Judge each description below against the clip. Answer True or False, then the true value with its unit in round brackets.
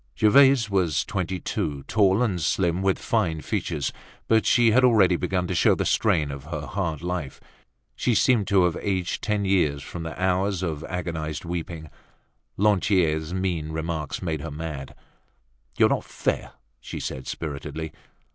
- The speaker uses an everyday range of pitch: True (3.9 semitones)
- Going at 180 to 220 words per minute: False (155 wpm)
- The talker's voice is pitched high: False (90 Hz)